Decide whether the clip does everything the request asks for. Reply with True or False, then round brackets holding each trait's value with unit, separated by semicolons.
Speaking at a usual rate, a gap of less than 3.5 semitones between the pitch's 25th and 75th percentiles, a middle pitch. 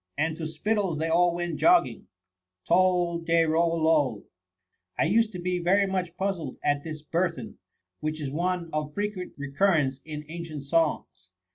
True (160 wpm; 2.9 semitones; 165 Hz)